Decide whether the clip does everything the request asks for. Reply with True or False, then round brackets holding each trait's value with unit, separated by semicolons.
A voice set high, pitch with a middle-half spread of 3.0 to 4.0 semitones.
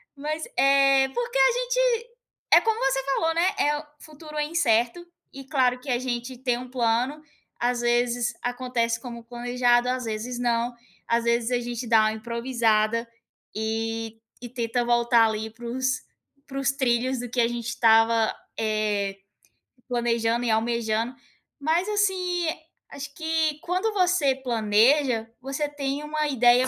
True (245 Hz; 3.3 semitones)